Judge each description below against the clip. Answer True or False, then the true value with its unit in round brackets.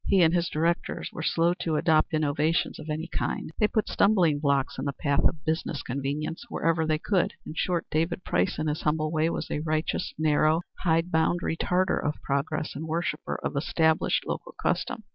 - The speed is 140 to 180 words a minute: False (190 wpm)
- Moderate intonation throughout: False (1.9 semitones)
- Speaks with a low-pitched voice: False (160 Hz)